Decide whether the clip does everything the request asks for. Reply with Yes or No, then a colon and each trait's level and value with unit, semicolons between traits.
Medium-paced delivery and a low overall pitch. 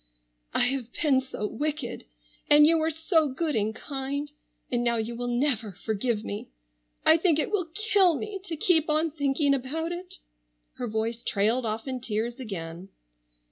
No: average, 155 wpm; very high, 265 Hz